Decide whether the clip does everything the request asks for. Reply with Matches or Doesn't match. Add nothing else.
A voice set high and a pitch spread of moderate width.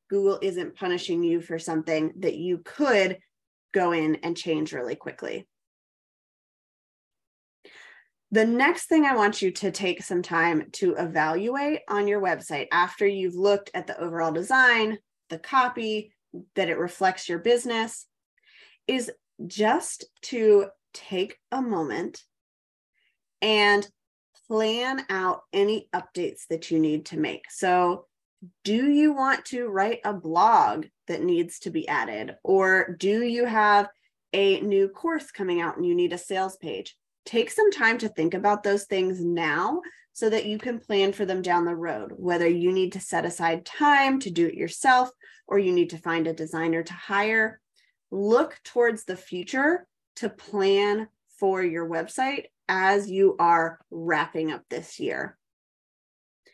Matches